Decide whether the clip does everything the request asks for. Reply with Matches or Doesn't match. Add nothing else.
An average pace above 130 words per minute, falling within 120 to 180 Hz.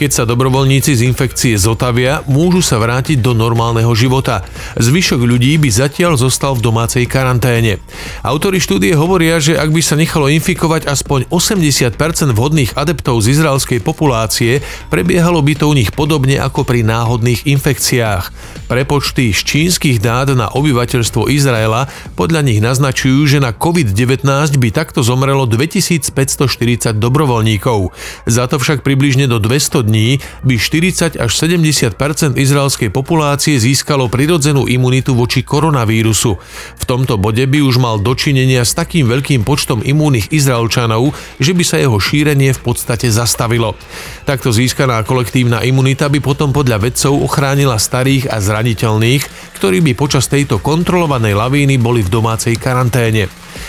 Matches